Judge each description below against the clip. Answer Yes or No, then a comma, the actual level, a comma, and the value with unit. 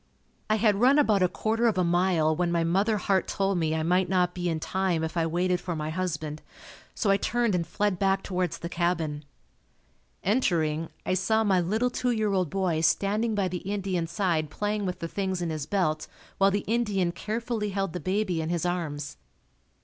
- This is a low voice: No, medium, 185 Hz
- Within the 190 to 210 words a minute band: Yes, fast, 205 wpm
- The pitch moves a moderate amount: Yes, average, 3.4 semitones